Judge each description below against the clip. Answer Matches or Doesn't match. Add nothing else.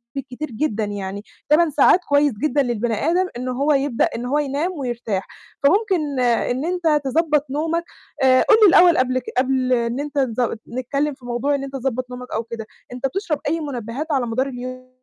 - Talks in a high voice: Matches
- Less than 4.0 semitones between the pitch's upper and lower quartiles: Matches